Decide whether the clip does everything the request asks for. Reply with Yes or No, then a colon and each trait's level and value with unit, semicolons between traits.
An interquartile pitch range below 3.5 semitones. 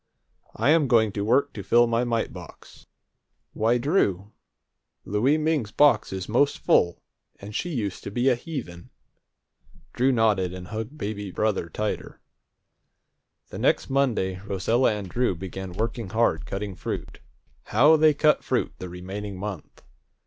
No: average, 4.8 semitones